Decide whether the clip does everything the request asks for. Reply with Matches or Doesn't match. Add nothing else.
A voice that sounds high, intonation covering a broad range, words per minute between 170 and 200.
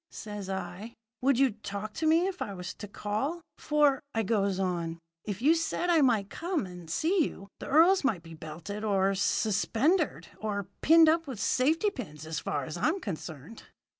Matches